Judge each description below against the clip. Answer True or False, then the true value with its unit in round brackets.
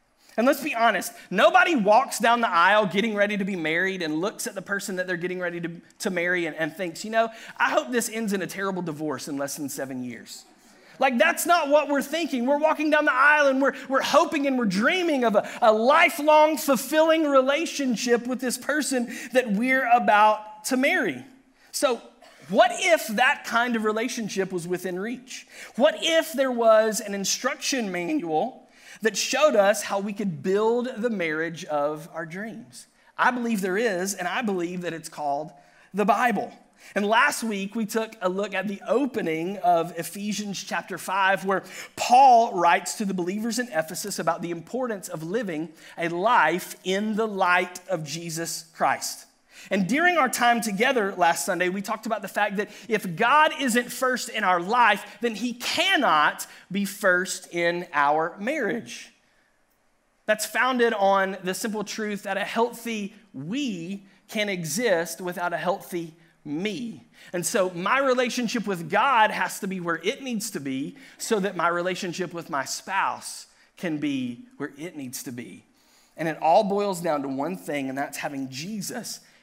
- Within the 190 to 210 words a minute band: False (180 wpm)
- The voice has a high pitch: True (210 Hz)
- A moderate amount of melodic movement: False (5.7 semitones)